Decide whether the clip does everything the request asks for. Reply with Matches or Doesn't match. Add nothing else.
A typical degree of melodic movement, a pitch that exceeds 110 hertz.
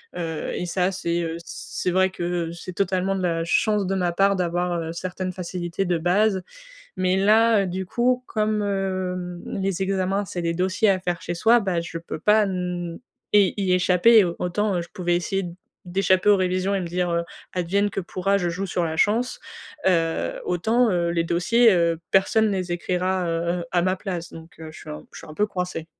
Doesn't match